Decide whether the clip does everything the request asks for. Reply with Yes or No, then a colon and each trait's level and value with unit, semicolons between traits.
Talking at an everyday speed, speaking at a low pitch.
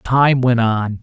Yes: average, 175 wpm; low, 120 Hz